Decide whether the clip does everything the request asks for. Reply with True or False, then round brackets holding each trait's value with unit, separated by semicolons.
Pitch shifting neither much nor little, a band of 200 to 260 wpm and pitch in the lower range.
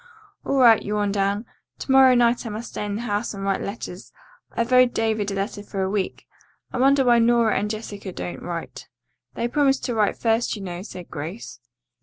False (3.3 semitones; 205 wpm; 215 Hz)